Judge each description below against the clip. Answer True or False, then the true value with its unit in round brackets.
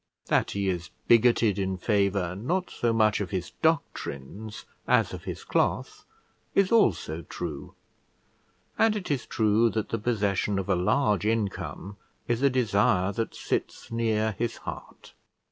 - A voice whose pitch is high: False (110 Hz)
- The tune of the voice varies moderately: True (3.4 semitones)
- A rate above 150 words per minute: False (145 wpm)